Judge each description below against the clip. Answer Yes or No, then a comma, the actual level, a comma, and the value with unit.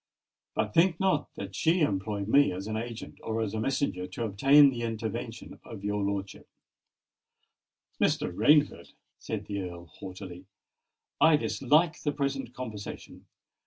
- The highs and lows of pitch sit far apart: Yes, wide, 6.2 semitones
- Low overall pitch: Yes, low, 110 Hz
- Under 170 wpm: Yes, average, 140 wpm